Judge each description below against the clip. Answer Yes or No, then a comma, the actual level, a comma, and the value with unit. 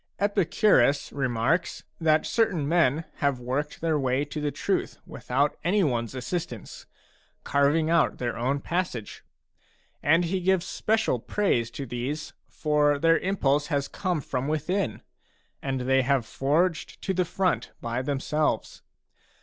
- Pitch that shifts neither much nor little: Yes, average, 4.3 semitones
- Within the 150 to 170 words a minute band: No, average, 140 wpm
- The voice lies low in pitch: No, medium, 150 Hz